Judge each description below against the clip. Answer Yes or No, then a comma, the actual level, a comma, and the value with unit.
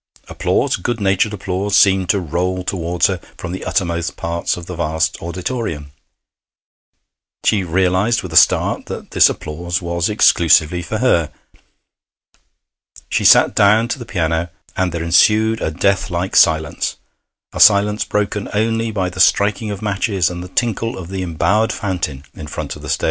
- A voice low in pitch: Yes, very low, 95 Hz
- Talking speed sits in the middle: Yes, average, 165 wpm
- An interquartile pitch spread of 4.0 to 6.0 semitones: No, average, 3.4 semitones